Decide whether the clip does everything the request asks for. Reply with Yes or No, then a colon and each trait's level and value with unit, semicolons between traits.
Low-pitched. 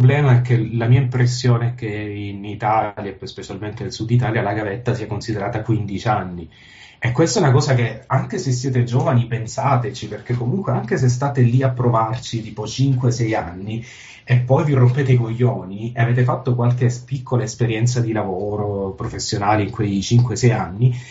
Yes: low, 120 Hz